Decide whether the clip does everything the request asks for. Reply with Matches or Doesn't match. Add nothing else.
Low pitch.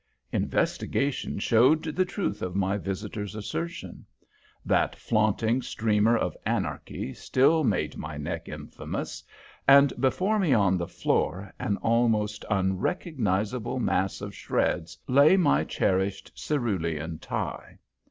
Matches